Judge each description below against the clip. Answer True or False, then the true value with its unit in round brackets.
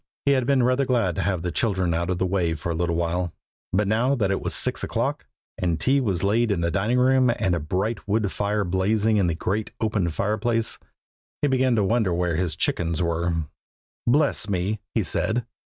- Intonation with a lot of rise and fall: False (4.8 semitones)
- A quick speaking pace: True (210 wpm)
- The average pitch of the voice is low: True (100 Hz)